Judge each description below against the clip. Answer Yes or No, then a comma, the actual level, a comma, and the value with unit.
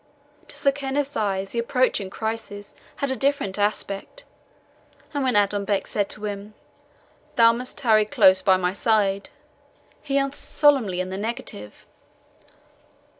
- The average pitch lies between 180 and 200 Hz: No, high, 215 Hz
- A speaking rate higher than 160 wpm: No, slow, 135 wpm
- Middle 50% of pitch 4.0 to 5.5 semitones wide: Yes, average, 4.9 semitones